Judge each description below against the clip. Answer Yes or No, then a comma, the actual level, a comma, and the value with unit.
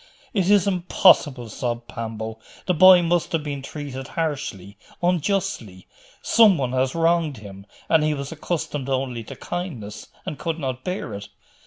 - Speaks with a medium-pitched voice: Yes, medium, 145 Hz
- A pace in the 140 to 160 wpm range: Yes, average, 155 wpm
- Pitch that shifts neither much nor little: No, wide, 6.3 semitones